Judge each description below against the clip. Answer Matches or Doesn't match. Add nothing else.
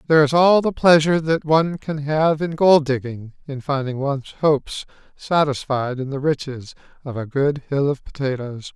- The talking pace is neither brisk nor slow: Matches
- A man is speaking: Matches